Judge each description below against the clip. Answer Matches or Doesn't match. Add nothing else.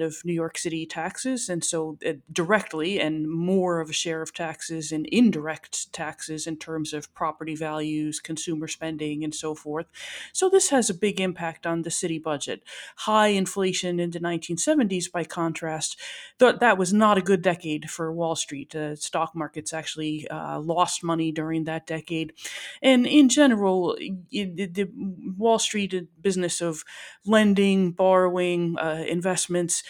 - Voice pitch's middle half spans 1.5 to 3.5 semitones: Matches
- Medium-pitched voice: Matches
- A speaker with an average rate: Matches